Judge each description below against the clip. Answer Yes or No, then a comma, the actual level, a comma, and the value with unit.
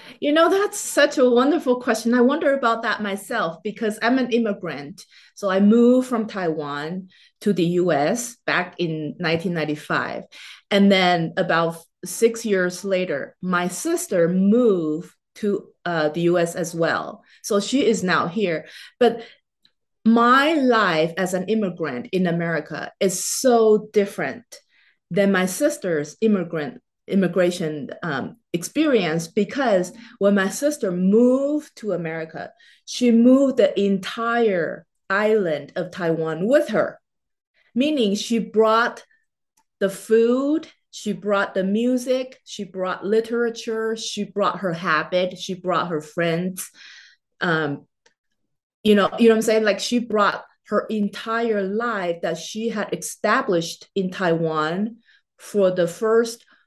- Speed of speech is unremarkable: No, slow, 130 wpm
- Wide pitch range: No, average, 4.8 semitones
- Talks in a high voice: Yes, high, 200 Hz